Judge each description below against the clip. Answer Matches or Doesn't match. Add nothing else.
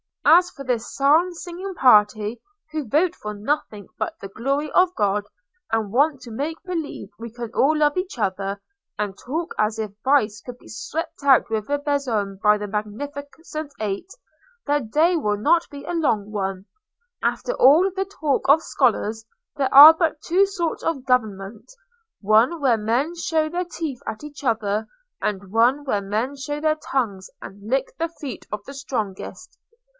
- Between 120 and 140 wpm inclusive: Doesn't match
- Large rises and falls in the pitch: Matches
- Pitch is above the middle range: Matches